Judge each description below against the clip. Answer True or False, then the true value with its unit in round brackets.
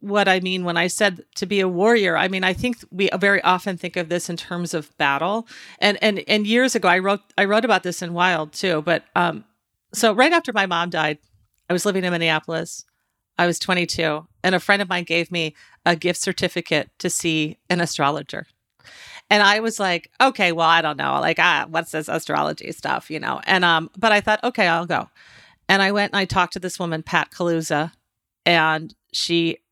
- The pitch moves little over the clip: False (3.2 semitones)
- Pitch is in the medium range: True (180 Hz)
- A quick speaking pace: True (215 wpm)